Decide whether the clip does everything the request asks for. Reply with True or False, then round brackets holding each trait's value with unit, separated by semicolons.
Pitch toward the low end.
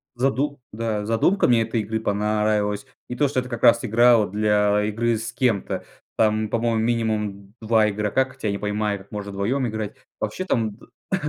True (110 Hz)